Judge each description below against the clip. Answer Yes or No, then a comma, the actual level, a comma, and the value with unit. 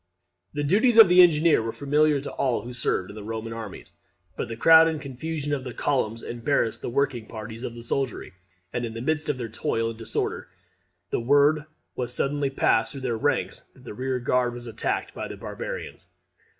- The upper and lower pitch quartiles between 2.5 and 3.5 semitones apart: No, average, 4.3 semitones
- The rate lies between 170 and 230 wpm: Yes, average, 200 wpm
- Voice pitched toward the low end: Yes, low, 125 Hz